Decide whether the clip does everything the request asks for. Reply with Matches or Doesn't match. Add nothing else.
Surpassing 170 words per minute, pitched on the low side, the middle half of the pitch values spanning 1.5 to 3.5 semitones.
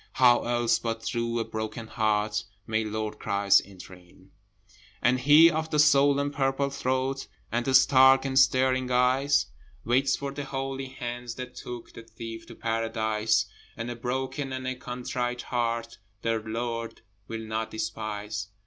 Doesn't match